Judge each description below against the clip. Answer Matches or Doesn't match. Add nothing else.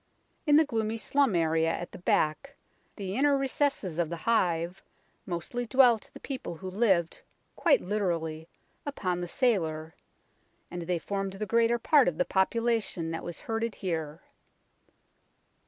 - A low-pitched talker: Doesn't match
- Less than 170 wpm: Matches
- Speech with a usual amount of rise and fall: Doesn't match